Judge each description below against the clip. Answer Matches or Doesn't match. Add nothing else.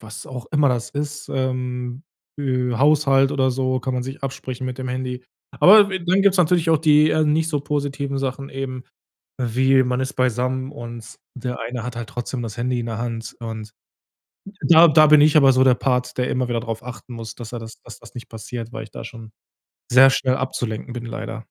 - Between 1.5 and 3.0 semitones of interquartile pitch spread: Matches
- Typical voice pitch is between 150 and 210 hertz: Doesn't match